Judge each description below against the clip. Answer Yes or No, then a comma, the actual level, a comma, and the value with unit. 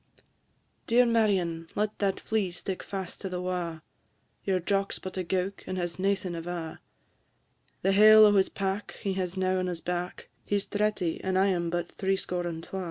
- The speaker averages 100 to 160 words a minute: No, average, 190 wpm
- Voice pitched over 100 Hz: Yes, medium, 185 Hz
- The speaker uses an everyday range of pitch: No, narrow, 2.0 semitones